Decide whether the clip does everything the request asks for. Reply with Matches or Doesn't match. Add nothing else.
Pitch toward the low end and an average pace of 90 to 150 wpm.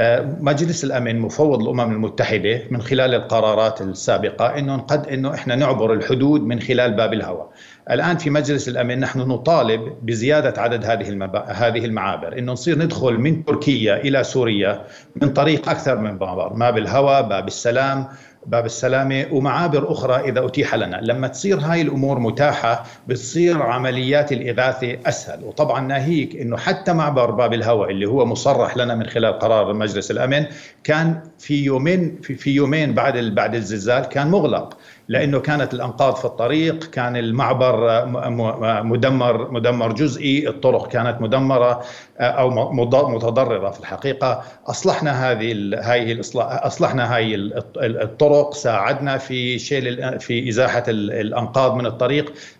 Matches